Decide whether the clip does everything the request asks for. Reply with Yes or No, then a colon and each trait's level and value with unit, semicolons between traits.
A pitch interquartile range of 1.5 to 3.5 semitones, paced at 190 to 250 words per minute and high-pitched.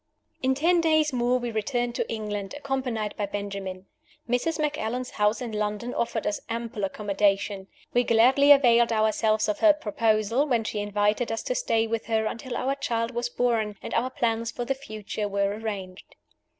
No: average, 3.0 semitones; average, 175 wpm; high, 230 Hz